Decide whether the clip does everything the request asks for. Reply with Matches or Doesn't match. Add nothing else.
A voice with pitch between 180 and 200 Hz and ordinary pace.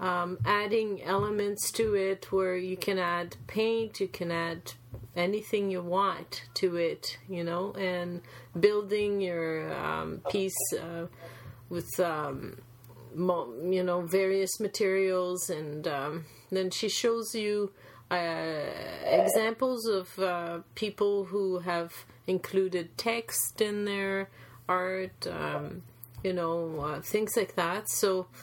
Doesn't match